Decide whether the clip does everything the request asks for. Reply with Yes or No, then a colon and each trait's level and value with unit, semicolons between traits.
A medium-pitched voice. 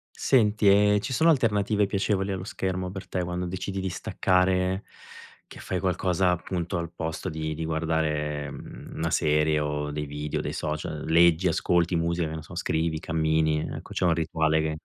No: very low, 85 Hz